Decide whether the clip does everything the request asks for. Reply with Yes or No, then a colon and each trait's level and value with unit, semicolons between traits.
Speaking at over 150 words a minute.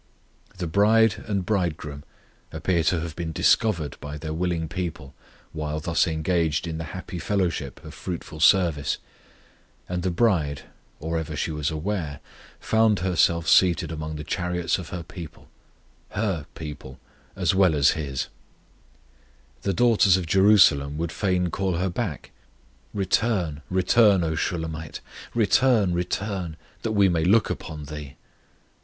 No: average, 140 wpm